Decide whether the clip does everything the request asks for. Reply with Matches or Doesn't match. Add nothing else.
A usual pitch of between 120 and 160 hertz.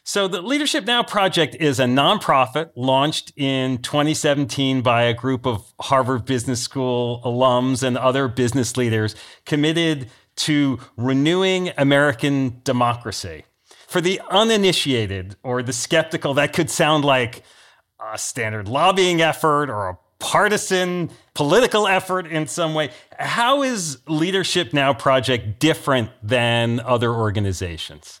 Matches